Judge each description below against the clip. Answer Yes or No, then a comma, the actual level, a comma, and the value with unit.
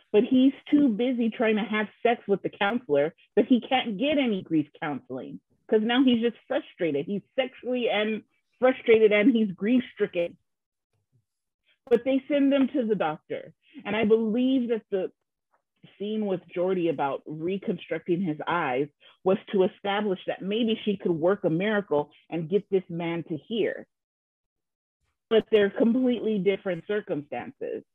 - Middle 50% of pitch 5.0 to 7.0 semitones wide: Yes, average, 5.3 semitones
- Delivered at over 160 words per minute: No, average, 150 wpm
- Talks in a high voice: Yes, high, 210 Hz